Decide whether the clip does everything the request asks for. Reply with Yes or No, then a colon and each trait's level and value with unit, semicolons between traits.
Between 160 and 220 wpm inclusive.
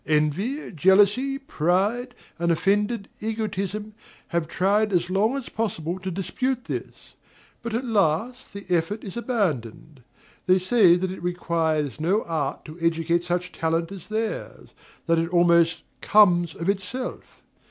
No: average, 140 wpm